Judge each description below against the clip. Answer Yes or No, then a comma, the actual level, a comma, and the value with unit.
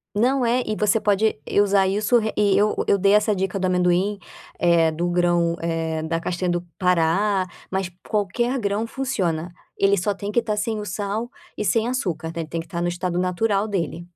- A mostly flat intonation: No, average, 3.3 semitones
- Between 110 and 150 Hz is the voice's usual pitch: No, high, 195 Hz